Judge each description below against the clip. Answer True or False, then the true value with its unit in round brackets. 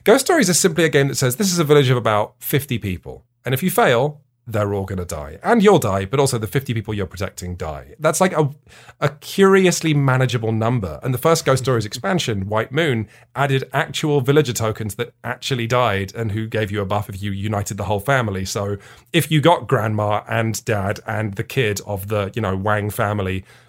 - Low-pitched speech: True (120 Hz)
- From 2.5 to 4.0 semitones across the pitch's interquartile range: False (5.4 semitones)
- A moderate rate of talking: False (220 wpm)